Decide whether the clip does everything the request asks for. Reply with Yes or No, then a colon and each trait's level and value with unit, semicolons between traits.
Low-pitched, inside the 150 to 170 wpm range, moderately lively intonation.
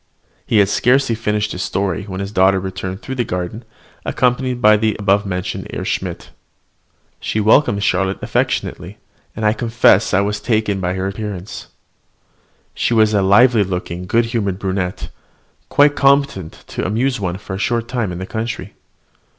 Yes: low, 105 Hz; average, 165 wpm; average, 3.4 semitones